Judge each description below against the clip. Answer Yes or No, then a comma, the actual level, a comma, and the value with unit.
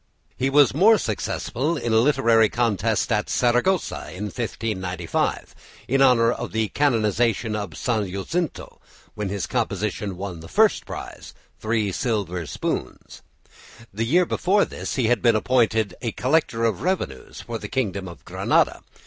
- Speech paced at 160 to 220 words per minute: No, average, 150 wpm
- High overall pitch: No, low, 115 Hz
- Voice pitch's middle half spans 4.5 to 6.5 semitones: No, average, 3.9 semitones